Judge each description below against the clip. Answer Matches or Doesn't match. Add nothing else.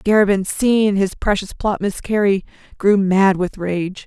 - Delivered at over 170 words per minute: Doesn't match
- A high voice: Matches